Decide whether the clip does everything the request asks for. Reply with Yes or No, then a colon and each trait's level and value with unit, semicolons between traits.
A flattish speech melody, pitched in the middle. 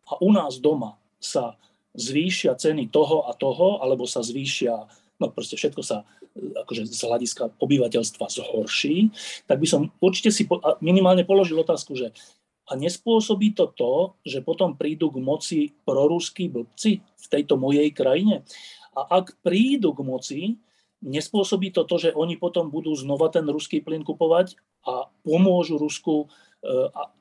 No: average, 5.0 semitones; medium, 165 Hz